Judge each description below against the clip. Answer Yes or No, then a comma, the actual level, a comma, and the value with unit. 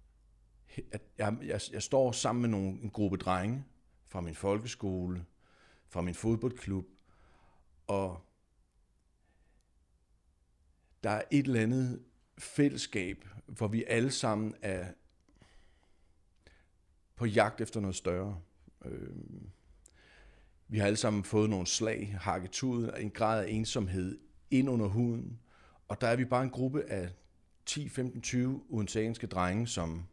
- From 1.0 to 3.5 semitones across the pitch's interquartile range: No, average, 4.9 semitones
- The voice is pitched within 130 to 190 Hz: No, low, 100 Hz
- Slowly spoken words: Yes, slow, 120 wpm